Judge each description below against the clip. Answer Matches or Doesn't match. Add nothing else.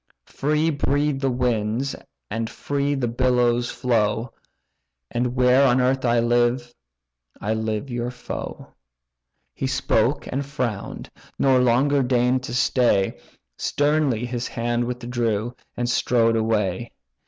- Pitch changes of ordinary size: Doesn't match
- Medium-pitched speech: Doesn't match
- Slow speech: Matches